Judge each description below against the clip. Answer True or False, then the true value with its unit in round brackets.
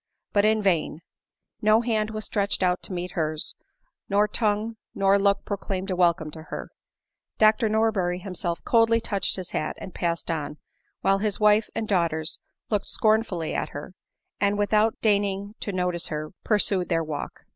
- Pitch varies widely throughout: False (3.4 semitones)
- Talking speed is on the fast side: False (165 wpm)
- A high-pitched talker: True (195 Hz)